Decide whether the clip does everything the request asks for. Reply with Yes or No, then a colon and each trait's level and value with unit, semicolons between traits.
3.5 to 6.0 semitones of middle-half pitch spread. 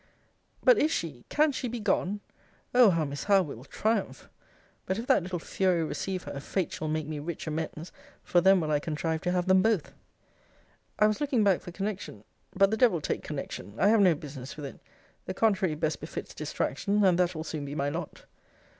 Yes: average, 4.7 semitones